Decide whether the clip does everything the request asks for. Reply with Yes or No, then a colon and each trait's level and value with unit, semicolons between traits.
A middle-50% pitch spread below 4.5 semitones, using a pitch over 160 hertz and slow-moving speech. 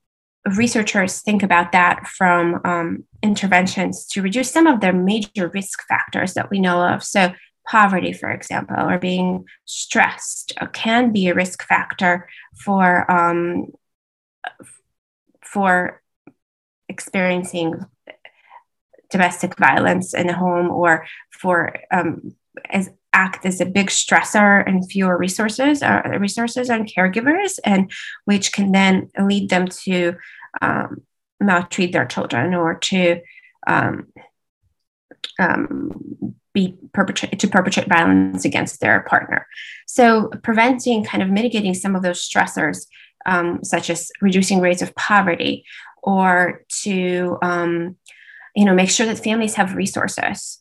Yes: narrow, 2.5 semitones; medium, 185 Hz; slow, 125 wpm